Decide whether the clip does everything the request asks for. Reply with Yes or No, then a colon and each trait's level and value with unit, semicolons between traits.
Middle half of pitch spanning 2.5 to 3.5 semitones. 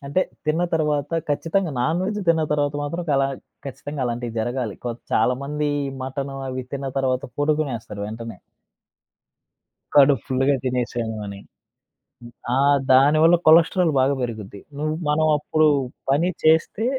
No: average, 3.9 semitones